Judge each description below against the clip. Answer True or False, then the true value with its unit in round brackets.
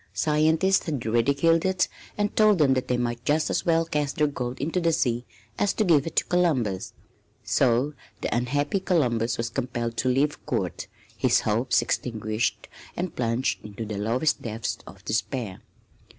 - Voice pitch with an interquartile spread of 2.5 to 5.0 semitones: False (5.5 semitones)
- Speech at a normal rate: True (165 wpm)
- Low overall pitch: True (130 Hz)